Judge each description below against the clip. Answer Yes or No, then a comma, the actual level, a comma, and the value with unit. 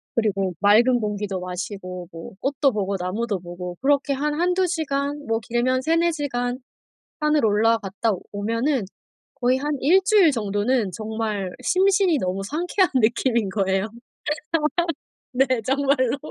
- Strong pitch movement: Yes, wide, 5.9 semitones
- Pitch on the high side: Yes, high, 235 Hz